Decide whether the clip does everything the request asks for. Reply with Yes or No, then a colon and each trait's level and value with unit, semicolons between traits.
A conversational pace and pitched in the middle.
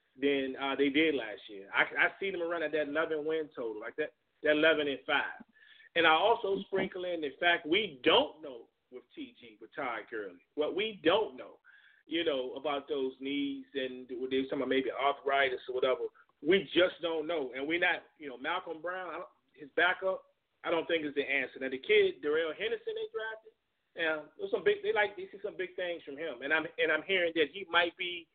No: fast, 220 wpm; medium, 175 Hz